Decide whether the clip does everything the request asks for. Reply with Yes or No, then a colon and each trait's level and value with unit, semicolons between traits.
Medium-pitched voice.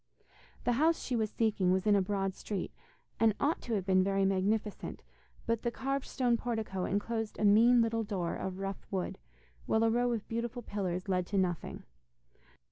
No: high, 210 Hz